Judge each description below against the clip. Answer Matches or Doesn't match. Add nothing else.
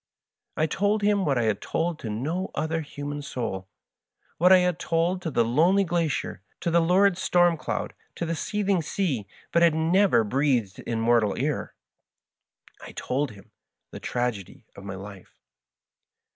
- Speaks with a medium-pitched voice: Matches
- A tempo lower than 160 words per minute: Doesn't match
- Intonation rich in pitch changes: Matches